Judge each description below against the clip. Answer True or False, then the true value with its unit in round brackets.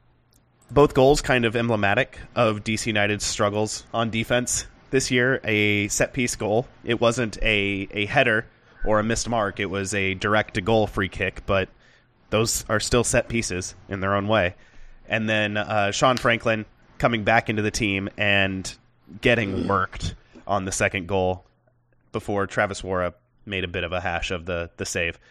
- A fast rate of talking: False (170 wpm)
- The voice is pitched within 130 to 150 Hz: False (105 Hz)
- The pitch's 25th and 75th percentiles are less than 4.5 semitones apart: True (2.8 semitones)